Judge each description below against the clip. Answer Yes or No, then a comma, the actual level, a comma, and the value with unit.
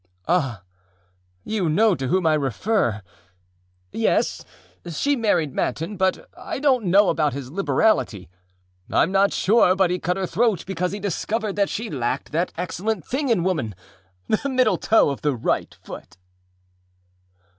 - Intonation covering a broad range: Yes, wide, 5.8 semitones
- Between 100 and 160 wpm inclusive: Yes, average, 155 wpm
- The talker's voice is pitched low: No, medium, 185 Hz